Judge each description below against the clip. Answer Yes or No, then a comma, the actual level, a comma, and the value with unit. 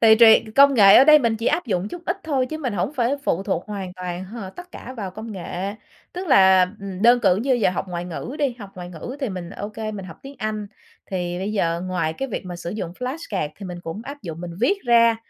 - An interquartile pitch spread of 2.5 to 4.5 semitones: No, wide, 5.5 semitones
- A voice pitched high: Yes, high, 210 Hz